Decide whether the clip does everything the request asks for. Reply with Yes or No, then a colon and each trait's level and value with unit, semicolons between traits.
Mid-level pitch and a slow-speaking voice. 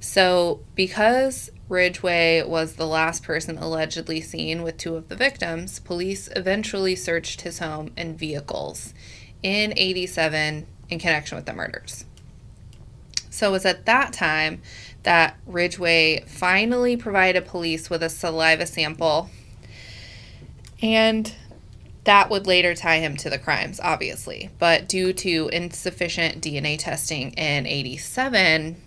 Yes: medium, 170 Hz; slow, 125 wpm